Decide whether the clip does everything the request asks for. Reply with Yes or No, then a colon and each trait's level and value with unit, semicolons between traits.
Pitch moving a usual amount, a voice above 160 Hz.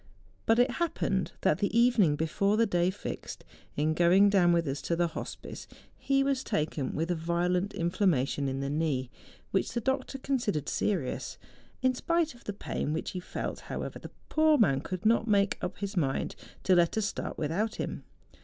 No: wide, 5.9 semitones; medium, 185 Hz